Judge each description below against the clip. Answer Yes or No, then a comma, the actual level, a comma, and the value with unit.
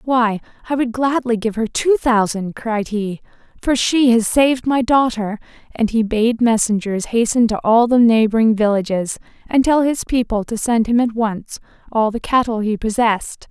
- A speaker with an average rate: Yes, average, 180 wpm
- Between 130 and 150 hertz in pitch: No, high, 230 Hz